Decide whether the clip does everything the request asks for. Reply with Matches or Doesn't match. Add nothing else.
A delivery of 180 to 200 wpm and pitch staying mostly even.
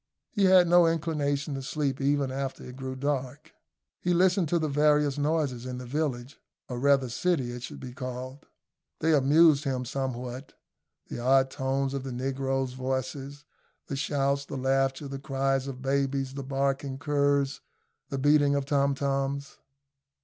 Doesn't match